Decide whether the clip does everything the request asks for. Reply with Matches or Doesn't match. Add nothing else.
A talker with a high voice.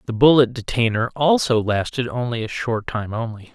Doesn't match